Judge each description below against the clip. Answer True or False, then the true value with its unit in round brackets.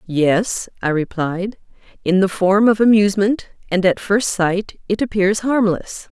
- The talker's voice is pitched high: True (195 Hz)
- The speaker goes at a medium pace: True (145 wpm)